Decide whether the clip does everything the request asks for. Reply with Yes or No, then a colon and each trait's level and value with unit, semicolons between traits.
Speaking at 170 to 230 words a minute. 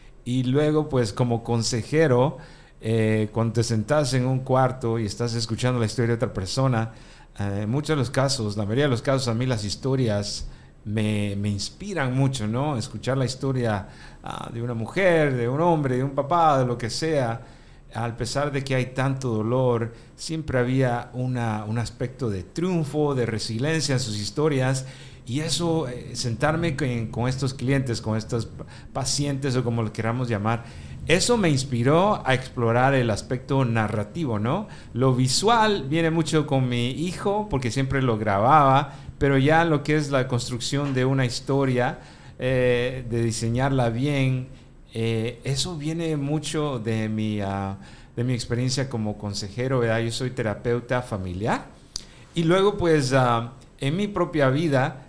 No: average, 160 wpm